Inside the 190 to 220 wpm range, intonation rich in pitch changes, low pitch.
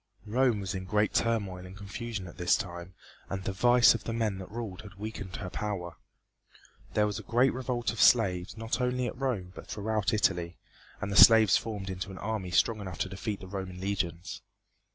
No: average, 200 wpm; average, 3.3 semitones; low, 100 Hz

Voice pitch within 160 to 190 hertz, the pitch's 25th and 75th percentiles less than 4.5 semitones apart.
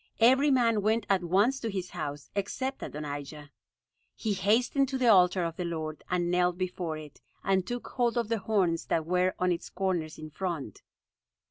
No: medium, 185 Hz; average, 5.2 semitones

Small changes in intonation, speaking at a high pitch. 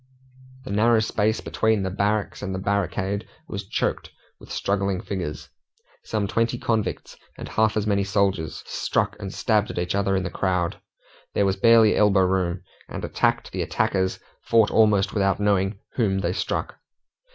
No: narrow, 2.1 semitones; low, 100 Hz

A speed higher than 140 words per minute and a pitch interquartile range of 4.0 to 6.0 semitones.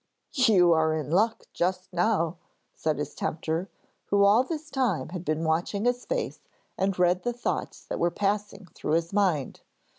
Yes: average, 170 wpm; average, 4.6 semitones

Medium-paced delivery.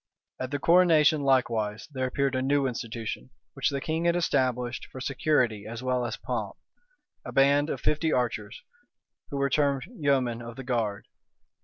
Yes: average, 165 wpm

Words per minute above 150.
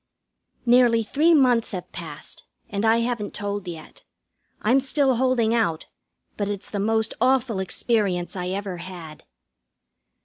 No: slow, 135 wpm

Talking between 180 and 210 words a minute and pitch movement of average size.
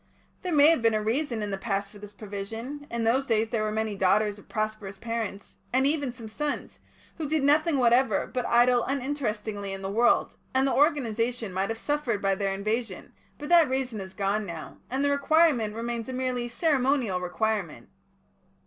Yes: average, 190 wpm; average, 4.4 semitones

